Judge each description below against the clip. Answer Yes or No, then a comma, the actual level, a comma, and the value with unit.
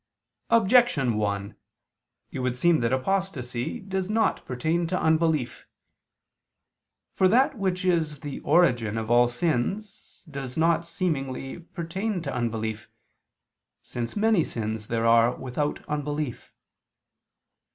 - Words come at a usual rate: No, slow, 115 wpm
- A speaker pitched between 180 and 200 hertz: No, medium, 150 Hz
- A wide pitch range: Yes, wide, 7.1 semitones